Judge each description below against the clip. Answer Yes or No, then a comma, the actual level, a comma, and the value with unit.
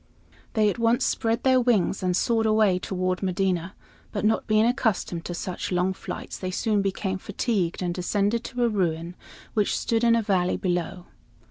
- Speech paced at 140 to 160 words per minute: No, average, 175 wpm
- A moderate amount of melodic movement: Yes, average, 3.6 semitones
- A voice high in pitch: Yes, high, 195 Hz